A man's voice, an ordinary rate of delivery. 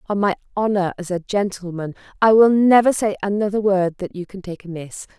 No: female; average, 195 wpm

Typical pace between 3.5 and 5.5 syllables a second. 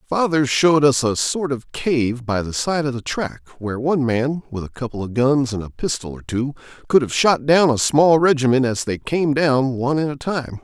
Yes: 5.1 syllables/s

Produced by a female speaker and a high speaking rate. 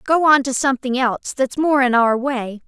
Yes: female; fast, 225 wpm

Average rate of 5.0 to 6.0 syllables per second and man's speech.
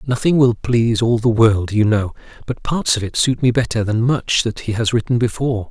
Yes: 5.3 syllables/s; male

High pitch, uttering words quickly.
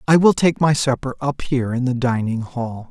No: low, 130 Hz; fast, 225 wpm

